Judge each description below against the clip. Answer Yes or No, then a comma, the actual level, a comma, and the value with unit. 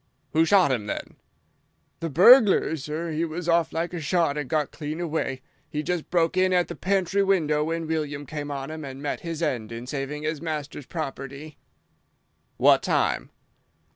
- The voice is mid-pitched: Yes, medium, 155 Hz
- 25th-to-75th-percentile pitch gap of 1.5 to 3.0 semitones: Yes, average, 2.7 semitones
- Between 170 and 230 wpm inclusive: Yes, average, 175 wpm